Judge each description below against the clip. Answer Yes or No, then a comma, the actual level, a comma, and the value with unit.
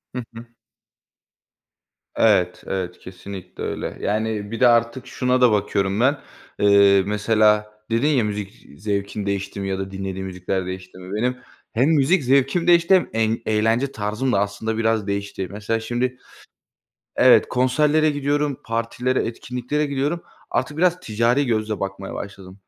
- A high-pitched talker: No, low, 110 Hz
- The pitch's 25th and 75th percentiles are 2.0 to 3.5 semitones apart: No, average, 4.3 semitones